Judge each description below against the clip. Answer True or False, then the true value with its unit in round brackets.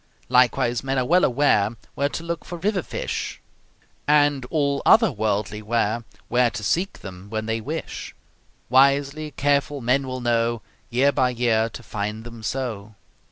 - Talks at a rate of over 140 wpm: True (160 wpm)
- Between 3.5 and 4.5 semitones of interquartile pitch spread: True (4.2 semitones)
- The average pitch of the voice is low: True (125 Hz)